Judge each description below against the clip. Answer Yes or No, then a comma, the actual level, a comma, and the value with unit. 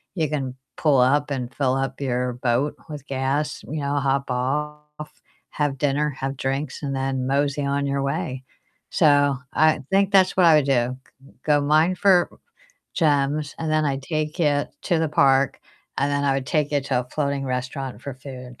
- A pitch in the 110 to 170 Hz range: Yes, medium, 140 Hz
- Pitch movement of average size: No, narrow, 2.1 semitones